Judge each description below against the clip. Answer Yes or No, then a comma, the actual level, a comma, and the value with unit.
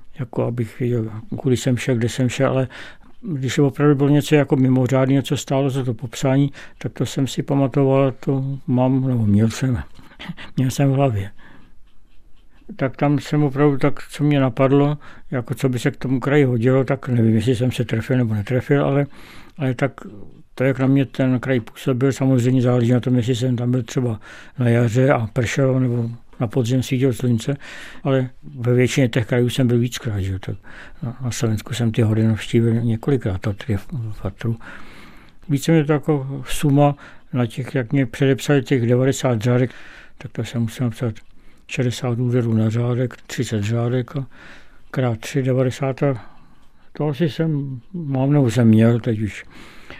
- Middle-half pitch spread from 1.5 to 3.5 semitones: Yes, narrow, 2.5 semitones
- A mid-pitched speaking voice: No, low, 130 Hz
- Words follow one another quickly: Yes, fast, 175 wpm